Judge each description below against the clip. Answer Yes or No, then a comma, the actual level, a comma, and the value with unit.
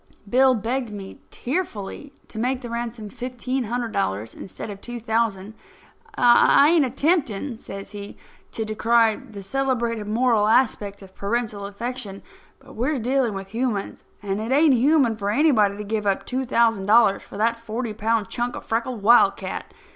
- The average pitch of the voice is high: Yes, high, 230 Hz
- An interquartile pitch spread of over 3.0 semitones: Yes, average, 3.4 semitones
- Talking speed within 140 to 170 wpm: Yes, average, 160 wpm